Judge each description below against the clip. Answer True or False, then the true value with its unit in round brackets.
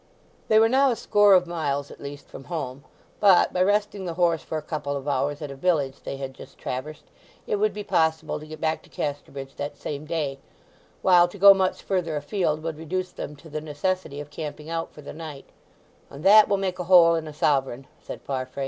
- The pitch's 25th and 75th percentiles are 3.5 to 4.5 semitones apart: True (4.2 semitones)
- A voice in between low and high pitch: True (160 Hz)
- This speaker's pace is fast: True (220 wpm)